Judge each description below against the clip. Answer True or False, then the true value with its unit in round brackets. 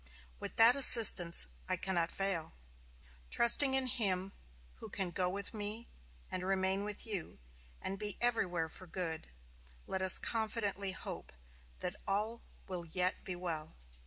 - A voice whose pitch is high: True (195 Hz)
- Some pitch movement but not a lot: True (3.2 semitones)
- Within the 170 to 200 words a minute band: False (140 wpm)